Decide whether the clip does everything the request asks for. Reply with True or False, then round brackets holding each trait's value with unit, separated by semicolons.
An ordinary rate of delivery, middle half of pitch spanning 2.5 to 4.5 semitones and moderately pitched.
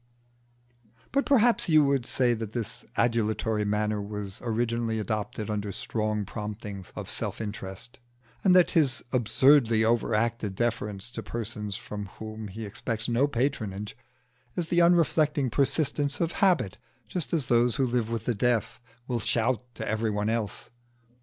False (145 wpm; 3.5 semitones; 115 Hz)